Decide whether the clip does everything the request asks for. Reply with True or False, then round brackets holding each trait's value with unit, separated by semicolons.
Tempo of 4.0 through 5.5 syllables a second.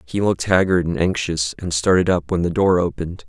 False (5.8 syllables/s)